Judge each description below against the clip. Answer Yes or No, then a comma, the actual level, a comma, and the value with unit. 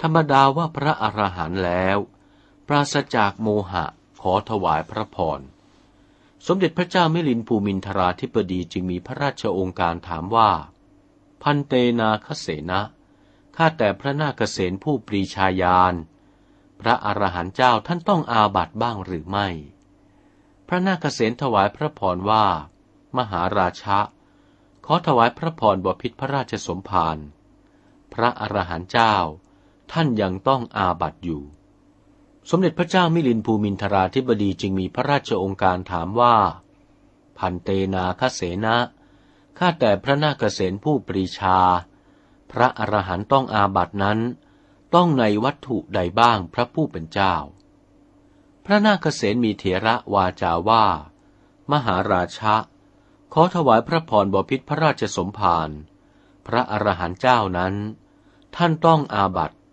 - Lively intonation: Yes, wide, 6.1 semitones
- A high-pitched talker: No, low, 105 Hz